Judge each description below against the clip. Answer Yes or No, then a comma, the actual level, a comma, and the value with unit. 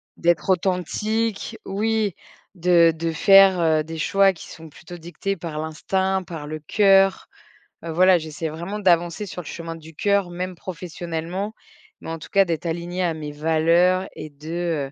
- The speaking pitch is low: No, medium, 175 Hz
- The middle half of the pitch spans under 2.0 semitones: No, average, 2.8 semitones